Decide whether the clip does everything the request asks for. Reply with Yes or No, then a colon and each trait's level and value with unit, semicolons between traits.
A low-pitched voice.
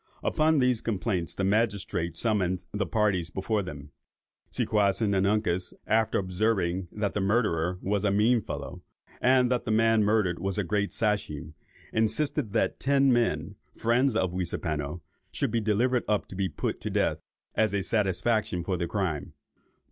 Yes: low, 105 Hz